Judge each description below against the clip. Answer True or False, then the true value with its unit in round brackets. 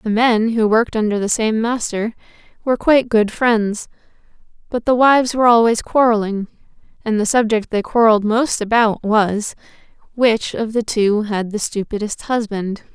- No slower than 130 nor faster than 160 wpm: True (155 wpm)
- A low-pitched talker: False (220 Hz)